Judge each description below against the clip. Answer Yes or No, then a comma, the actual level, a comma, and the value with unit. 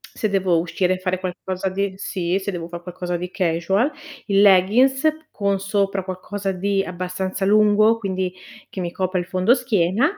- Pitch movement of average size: No, narrow, 1.9 semitones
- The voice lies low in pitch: No, high, 190 Hz